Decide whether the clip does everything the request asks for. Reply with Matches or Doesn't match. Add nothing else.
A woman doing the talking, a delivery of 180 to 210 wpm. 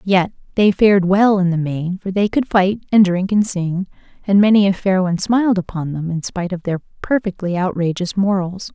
Matches